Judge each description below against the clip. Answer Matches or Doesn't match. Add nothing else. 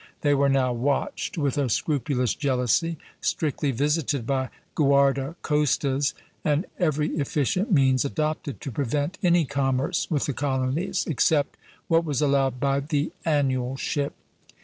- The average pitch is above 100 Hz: Matches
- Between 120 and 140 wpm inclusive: Matches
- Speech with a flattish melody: Matches